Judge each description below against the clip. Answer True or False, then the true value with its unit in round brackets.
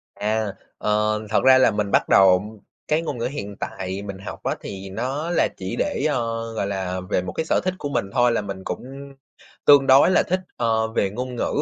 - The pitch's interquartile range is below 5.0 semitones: True (4.6 semitones)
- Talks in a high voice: False (110 Hz)